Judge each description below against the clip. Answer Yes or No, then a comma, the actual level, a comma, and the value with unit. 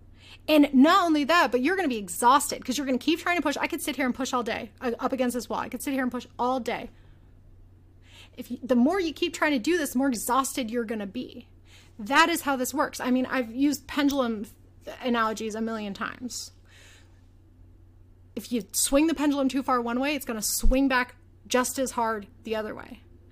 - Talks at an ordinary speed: No, fast, 220 wpm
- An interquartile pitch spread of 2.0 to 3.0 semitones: No, average, 4.4 semitones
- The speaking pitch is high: Yes, very high, 250 Hz